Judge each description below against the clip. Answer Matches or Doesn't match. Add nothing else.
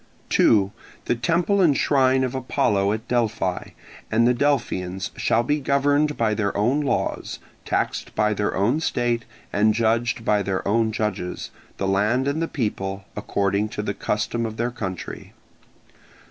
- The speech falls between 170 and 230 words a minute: Doesn't match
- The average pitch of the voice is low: Matches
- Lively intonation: Doesn't match